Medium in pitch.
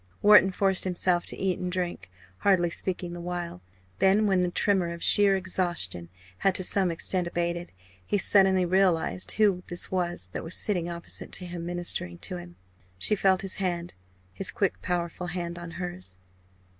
Yes: medium, 180 Hz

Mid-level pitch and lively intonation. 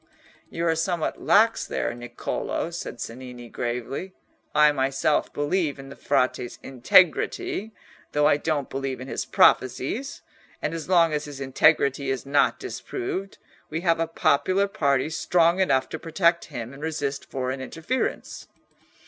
No: medium, 150 Hz; average, 4.1 semitones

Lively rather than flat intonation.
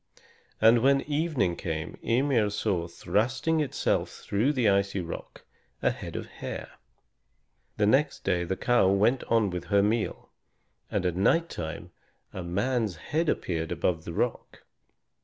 Yes: wide, 6.3 semitones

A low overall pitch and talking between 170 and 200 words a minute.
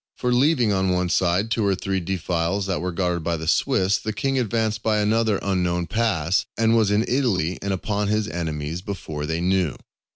Yes: very low, 95 Hz; average, 195 wpm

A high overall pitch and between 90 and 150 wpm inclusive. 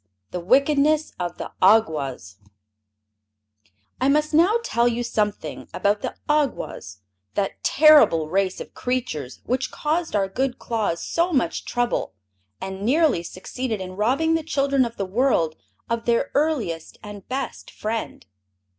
Yes: high, 235 Hz; slow, 135 wpm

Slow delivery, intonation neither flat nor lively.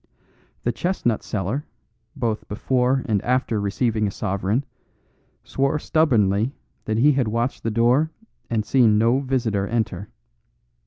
Yes: slow, 125 wpm; average, 3.7 semitones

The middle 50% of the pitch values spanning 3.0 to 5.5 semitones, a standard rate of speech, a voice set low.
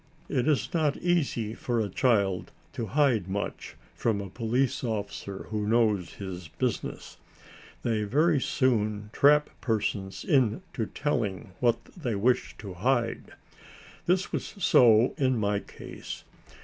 No: average, 4.4 semitones; slow, 130 wpm; low, 115 Hz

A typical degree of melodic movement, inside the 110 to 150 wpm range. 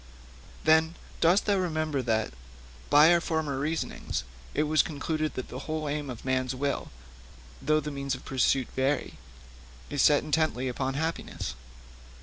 Yes: average, 3.0 semitones; average, 145 wpm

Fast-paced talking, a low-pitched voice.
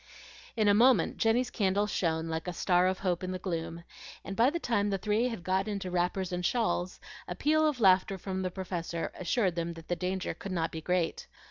No: fast, 220 wpm; medium, 185 Hz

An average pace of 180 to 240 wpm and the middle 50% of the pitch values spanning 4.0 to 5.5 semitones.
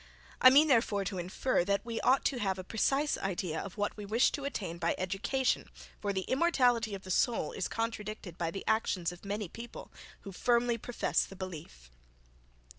Yes: average, 190 wpm; average, 4.3 semitones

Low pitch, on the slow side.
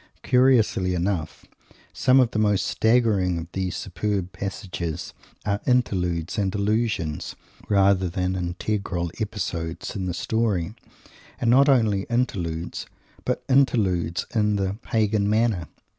Yes: low, 100 Hz; slow, 120 wpm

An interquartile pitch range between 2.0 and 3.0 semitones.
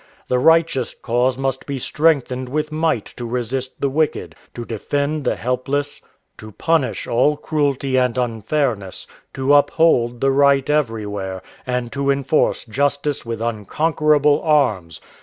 No: average, 3.6 semitones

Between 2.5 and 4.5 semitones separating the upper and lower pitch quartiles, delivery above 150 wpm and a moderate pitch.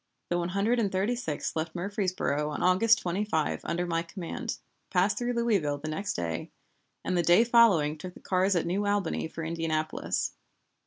Yes: average, 4.1 semitones; average, 175 wpm; medium, 180 Hz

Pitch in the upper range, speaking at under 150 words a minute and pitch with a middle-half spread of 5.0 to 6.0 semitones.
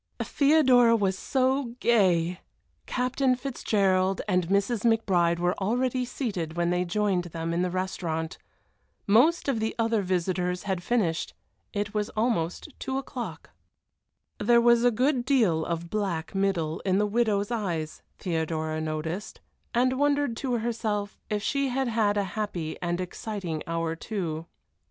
Yes: high, 205 Hz; average, 140 wpm; wide, 5.5 semitones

